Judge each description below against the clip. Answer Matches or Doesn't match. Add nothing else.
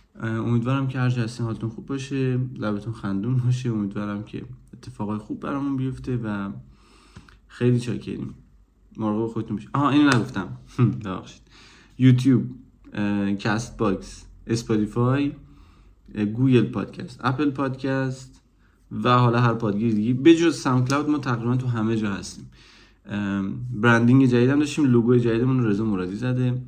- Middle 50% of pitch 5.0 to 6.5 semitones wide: Doesn't match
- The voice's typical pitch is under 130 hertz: Matches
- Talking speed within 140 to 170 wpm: Doesn't match